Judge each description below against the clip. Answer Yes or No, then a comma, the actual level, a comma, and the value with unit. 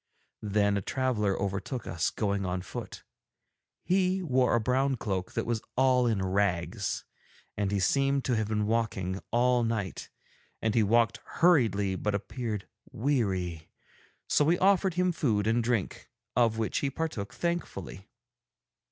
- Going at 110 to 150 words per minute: Yes, average, 145 wpm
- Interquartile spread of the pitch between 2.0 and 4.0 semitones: No, average, 4.6 semitones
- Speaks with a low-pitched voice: Yes, low, 110 Hz